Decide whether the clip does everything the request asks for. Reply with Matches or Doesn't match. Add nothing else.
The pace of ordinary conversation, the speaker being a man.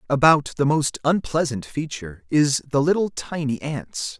Matches